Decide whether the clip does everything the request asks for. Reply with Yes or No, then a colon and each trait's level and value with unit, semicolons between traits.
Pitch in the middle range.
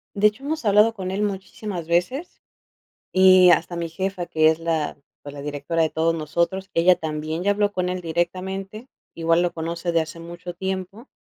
Yes: medium, 175 Hz